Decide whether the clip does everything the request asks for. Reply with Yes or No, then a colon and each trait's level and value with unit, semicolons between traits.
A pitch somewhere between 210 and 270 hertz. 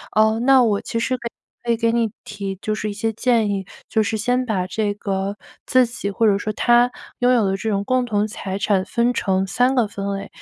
Yes: high, 215 Hz